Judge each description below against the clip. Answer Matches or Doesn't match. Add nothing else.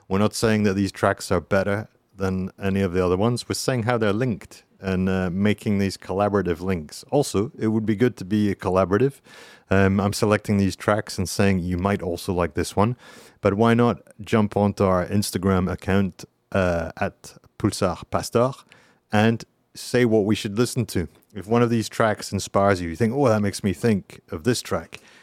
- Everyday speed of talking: Matches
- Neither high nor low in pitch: Doesn't match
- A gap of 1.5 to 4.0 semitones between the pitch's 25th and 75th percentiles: Matches